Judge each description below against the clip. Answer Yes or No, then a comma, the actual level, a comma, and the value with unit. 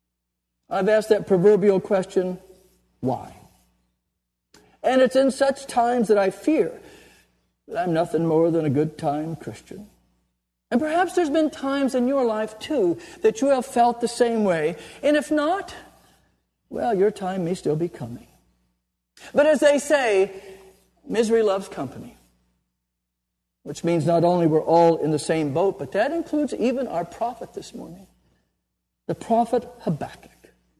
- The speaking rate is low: No, average, 150 wpm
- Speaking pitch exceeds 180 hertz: Yes, high, 190 Hz